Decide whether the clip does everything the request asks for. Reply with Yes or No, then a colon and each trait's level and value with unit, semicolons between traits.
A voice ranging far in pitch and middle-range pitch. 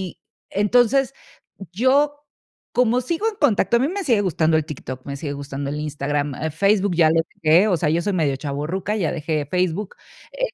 Yes: wide, 8.0 semitones; medium, 180 Hz